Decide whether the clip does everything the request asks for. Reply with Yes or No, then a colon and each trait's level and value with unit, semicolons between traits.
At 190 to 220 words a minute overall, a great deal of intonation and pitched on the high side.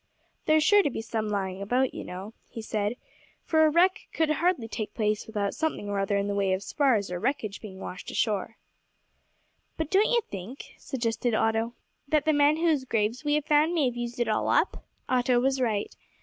Yes: fast, 205 wpm; wide, 6.1 semitones; high, 235 Hz